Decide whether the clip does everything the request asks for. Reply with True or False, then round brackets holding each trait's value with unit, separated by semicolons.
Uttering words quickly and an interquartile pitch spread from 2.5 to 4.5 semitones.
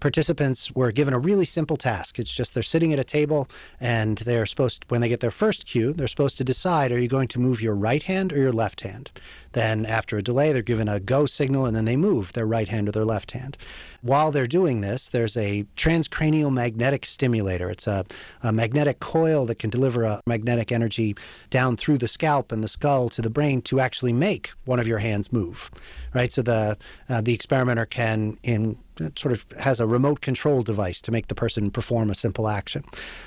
True (220 wpm; 3.8 semitones)